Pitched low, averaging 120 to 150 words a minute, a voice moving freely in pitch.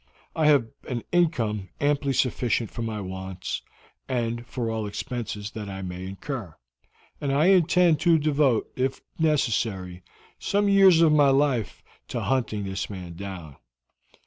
Yes: low, 120 Hz; average, 145 wpm; wide, 6.8 semitones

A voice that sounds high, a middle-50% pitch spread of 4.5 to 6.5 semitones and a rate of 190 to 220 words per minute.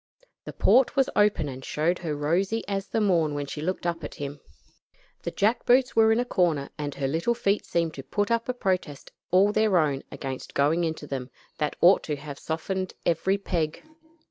No: medium, 170 Hz; average, 5.3 semitones; average, 200 wpm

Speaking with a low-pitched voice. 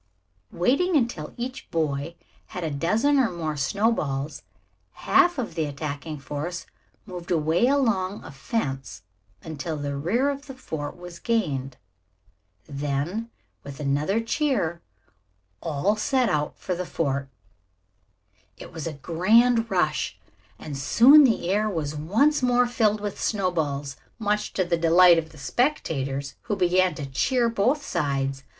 No: medium, 175 Hz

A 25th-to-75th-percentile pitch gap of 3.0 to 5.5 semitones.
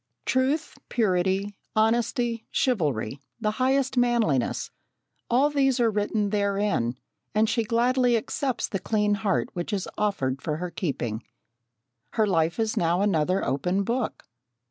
Yes: average, 5.0 semitones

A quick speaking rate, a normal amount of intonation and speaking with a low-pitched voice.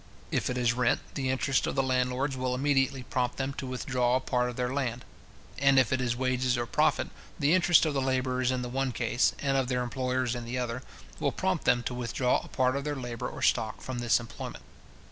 No: fast, 230 wpm; narrow, 1.4 semitones; low, 125 Hz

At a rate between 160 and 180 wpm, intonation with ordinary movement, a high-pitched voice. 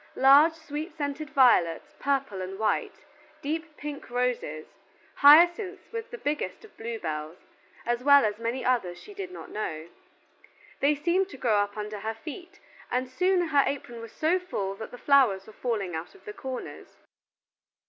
No: average, 170 wpm; wide, 6.7 semitones; very high, 265 Hz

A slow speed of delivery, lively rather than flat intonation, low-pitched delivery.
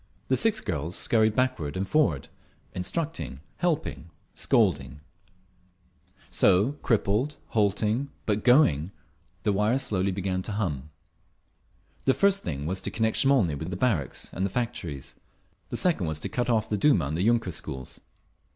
No: average, 145 wpm; wide, 6.4 semitones; low, 100 Hz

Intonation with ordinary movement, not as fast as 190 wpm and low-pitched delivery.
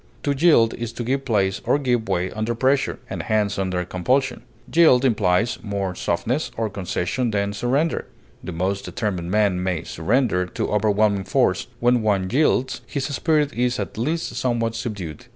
Yes: average, 4.9 semitones; average, 165 wpm; low, 110 Hz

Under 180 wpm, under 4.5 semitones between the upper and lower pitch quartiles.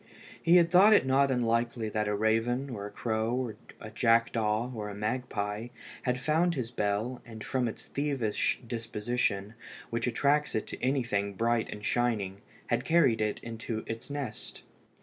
Yes: average, 165 wpm; average, 3.0 semitones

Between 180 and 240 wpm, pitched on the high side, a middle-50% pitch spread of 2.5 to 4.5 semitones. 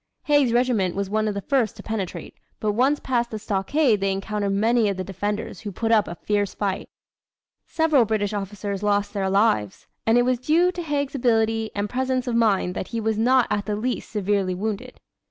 Yes: fast, 205 wpm; high, 215 Hz; average, 3.5 semitones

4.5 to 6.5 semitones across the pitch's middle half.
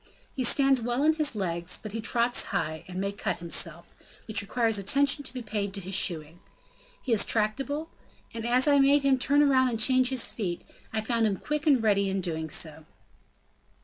Yes: wide, 5.5 semitones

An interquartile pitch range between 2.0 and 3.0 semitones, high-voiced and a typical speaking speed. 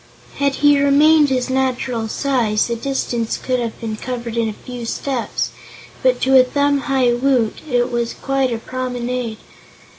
Yes: narrow, 2.5 semitones; very high, 250 Hz; average, 160 wpm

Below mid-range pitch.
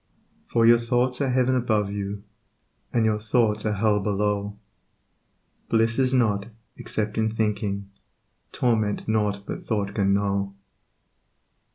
Yes: low, 105 Hz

